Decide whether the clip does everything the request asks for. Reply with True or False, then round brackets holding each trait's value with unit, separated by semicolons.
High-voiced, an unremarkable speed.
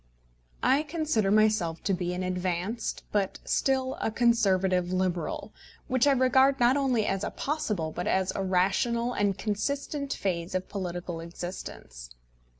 True (200 Hz; 145 wpm)